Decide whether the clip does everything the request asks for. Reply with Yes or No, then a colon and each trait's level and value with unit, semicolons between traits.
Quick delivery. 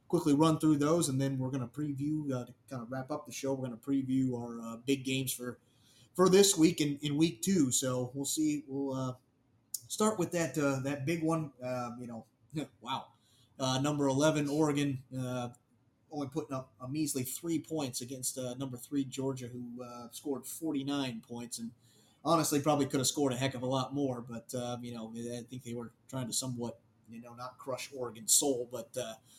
Yes: fast, 215 wpm